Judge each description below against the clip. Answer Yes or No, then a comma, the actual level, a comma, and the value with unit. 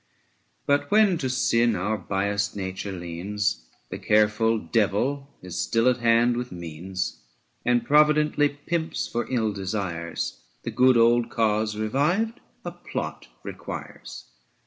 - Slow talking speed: Yes, slow, 130 wpm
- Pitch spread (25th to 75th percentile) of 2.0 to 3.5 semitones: No, average, 4.9 semitones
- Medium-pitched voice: No, low, 110 Hz